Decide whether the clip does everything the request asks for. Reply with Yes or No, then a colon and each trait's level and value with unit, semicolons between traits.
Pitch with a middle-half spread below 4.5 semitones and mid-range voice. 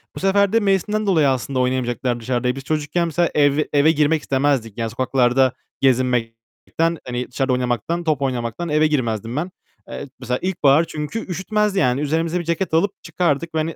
No: average, 4.9 semitones; medium, 145 Hz